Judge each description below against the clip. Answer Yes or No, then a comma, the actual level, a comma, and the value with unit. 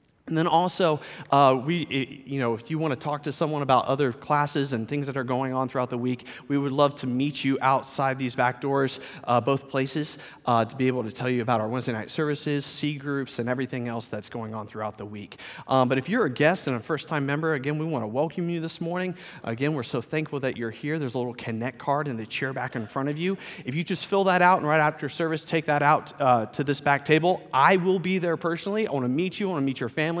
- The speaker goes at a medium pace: No, fast, 270 wpm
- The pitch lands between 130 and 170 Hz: Yes, medium, 140 Hz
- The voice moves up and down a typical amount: Yes, average, 3.8 semitones